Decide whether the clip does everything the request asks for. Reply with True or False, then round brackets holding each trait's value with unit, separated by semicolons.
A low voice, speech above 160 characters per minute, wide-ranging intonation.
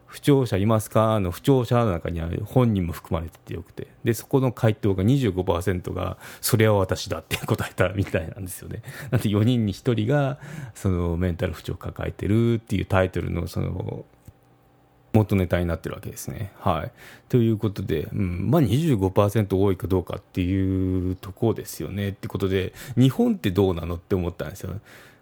False (100 Hz; 355 characters per minute; 4.0 semitones)